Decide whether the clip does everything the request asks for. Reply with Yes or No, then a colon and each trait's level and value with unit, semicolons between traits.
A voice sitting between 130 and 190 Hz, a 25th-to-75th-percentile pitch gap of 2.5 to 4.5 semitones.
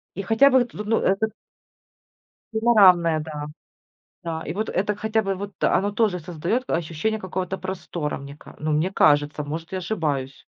No: medium, 185 Hz; average, 5.3 semitones